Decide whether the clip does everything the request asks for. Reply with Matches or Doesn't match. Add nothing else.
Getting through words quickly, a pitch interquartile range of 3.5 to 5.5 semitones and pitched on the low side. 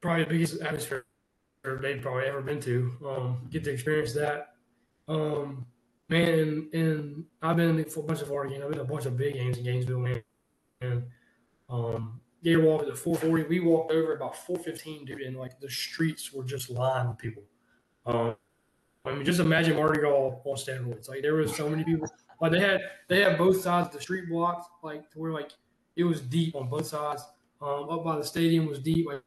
Doesn't match